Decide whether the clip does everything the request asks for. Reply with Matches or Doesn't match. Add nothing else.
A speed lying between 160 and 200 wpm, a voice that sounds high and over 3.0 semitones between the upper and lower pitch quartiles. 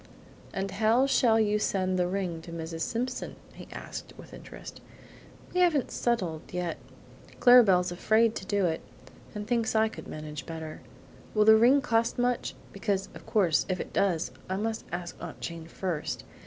Matches